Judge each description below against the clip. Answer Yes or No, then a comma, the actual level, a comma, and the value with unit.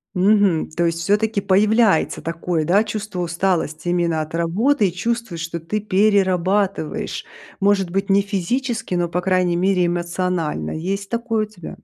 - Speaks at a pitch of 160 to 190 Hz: Yes, medium, 185 Hz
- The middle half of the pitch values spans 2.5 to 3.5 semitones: Yes, average, 3.2 semitones